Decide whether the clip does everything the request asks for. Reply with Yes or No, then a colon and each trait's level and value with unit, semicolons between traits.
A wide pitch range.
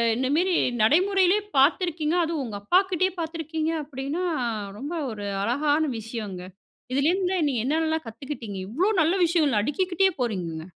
Yes: wide, 6.5 semitones